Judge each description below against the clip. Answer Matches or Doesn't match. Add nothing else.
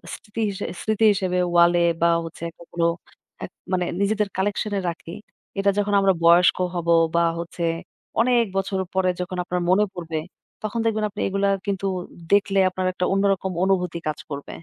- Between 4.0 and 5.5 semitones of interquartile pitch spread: Doesn't match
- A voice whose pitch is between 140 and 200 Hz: Matches